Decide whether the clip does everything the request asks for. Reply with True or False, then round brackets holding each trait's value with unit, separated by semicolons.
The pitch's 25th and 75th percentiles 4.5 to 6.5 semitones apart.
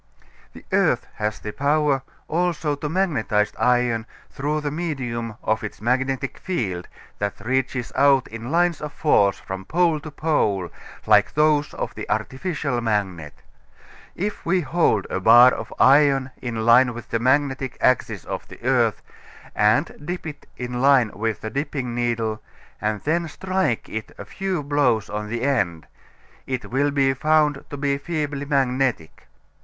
True (4.8 semitones)